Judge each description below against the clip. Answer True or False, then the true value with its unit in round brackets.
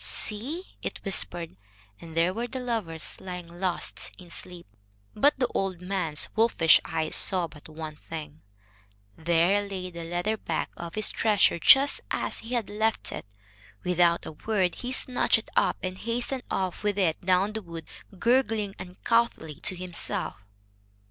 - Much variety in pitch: False (4.6 semitones)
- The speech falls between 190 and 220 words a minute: False (155 wpm)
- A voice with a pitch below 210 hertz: True (185 Hz)